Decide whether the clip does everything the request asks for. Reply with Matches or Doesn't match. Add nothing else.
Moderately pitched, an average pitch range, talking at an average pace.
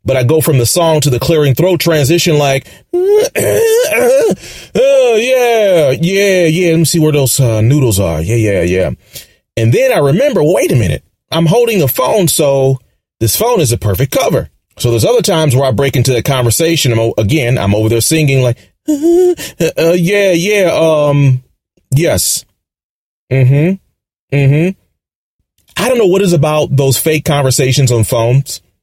Doesn't match